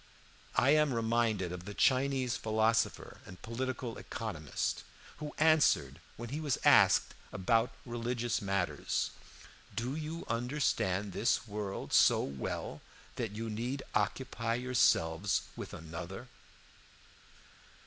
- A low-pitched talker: Yes, low, 115 Hz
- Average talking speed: No, slow, 110 wpm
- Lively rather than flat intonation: No, average, 4.3 semitones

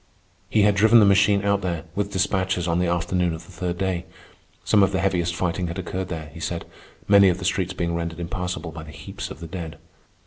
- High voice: No, very low, 90 Hz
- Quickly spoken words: Yes, fast, 230 wpm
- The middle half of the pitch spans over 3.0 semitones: No, narrow, 2.5 semitones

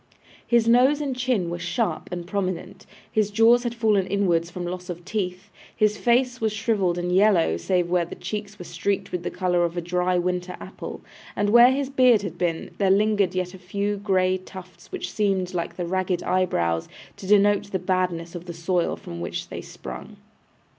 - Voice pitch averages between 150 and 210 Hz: Yes, medium, 185 Hz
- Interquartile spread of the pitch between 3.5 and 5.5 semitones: No, average, 3.0 semitones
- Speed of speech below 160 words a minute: No, average, 195 wpm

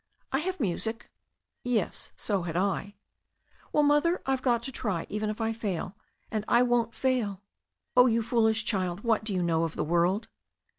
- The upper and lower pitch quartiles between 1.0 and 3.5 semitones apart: No, average, 4.3 semitones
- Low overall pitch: No, high, 220 Hz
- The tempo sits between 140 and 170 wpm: No, average, 180 wpm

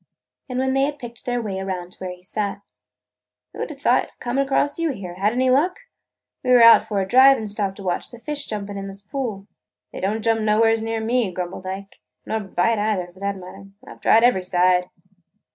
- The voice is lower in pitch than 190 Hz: No, high, 215 Hz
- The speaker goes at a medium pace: No, fast, 230 wpm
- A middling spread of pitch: Yes, average, 4.2 semitones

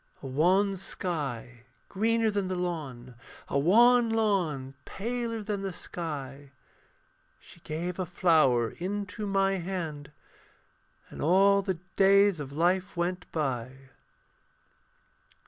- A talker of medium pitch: Yes, medium, 180 Hz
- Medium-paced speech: No, slow, 110 wpm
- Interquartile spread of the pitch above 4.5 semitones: Yes, average, 5.3 semitones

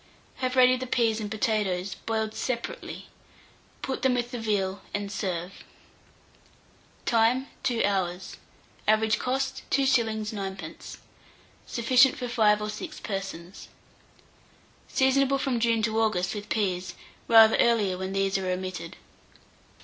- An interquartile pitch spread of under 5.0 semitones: Yes, average, 4.2 semitones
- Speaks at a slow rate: Yes, slow, 125 wpm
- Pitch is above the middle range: Yes, high, 220 Hz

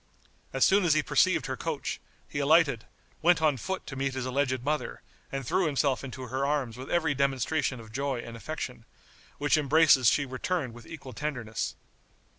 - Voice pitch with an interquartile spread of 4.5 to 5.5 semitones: No, average, 3.1 semitones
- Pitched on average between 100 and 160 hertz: Yes, low, 135 Hz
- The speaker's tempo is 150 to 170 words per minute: No, average, 180 wpm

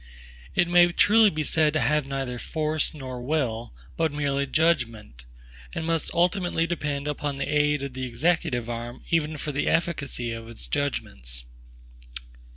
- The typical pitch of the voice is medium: Yes, medium, 145 Hz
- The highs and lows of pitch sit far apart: No, average, 4.4 semitones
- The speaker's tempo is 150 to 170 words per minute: Yes, average, 155 wpm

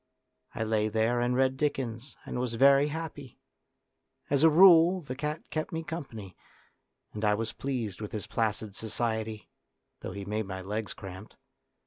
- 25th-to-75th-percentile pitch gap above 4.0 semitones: Yes, average, 4.8 semitones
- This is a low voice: Yes, low, 115 Hz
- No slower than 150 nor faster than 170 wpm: Yes, average, 160 wpm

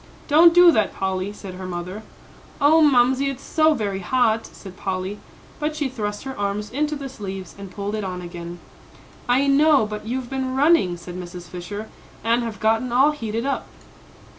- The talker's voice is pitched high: Yes, high, 220 Hz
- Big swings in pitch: Yes, wide, 6.1 semitones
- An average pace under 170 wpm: No, average, 180 wpm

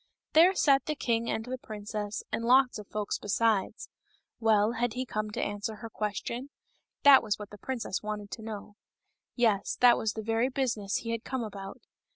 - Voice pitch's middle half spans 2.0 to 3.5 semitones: Yes, average, 2.9 semitones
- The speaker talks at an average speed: Yes, average, 190 wpm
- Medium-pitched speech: No, high, 225 Hz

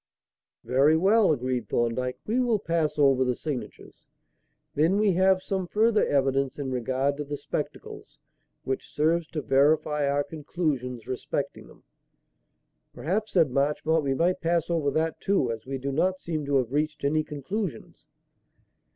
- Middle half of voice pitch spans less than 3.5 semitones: No, average, 4.1 semitones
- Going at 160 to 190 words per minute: No, average, 150 wpm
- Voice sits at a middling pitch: Yes, medium, 150 Hz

